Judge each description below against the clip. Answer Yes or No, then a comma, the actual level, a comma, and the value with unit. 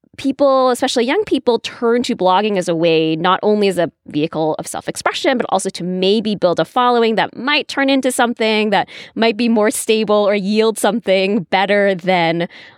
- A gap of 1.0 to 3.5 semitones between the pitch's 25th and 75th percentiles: No, average, 4.5 semitones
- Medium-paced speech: Yes, average, 190 wpm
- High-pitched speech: Yes, high, 210 Hz